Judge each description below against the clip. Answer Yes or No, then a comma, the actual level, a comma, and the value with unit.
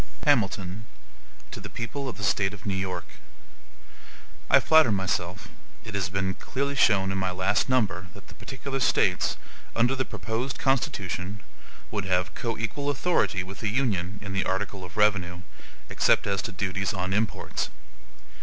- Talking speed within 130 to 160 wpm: Yes, average, 155 wpm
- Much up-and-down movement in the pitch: No, average, 3.7 semitones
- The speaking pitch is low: Yes, low, 100 Hz